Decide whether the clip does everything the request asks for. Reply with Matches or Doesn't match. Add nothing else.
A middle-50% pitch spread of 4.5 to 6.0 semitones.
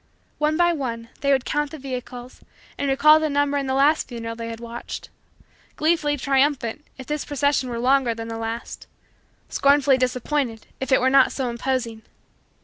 Doesn't match